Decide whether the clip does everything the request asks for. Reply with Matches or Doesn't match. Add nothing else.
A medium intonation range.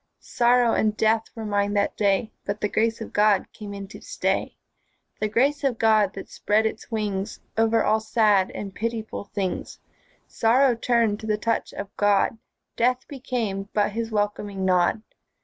Doesn't match